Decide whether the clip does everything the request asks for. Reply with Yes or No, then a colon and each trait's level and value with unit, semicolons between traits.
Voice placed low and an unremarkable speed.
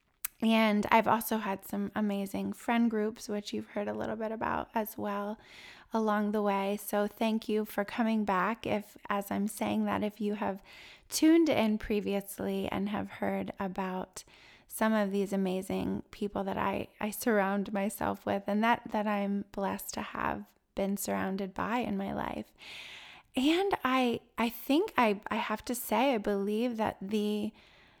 No: high, 210 Hz; average, 165 wpm